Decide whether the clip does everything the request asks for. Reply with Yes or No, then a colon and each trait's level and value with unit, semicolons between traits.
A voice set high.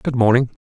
No: low, 125 Hz